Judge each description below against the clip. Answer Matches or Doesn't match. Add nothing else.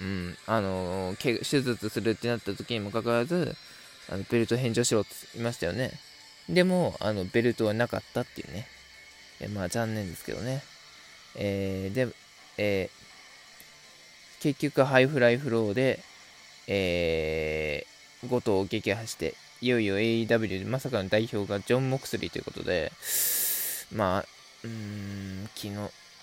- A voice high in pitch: Doesn't match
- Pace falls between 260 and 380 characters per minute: Matches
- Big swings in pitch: Doesn't match